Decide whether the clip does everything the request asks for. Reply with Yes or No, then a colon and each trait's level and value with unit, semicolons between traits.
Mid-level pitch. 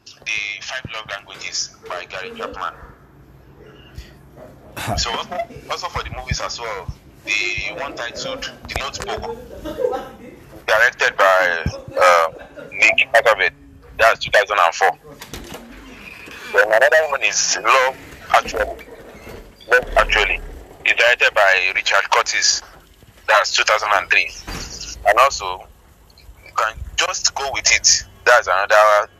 No: very low, 90 Hz